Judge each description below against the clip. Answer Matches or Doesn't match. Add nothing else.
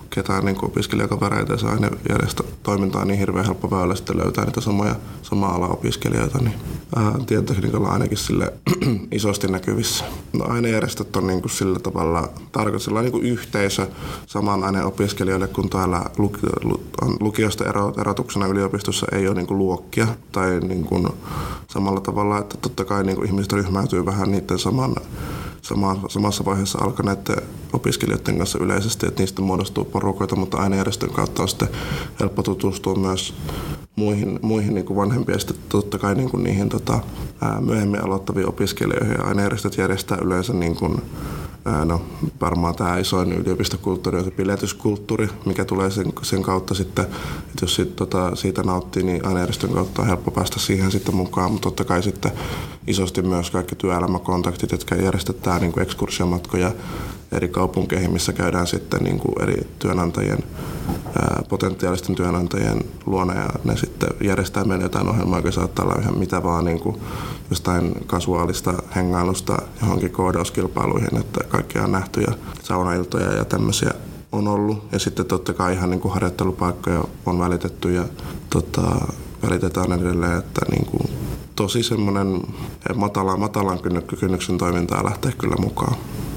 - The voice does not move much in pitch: Matches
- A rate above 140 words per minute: Matches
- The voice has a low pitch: Matches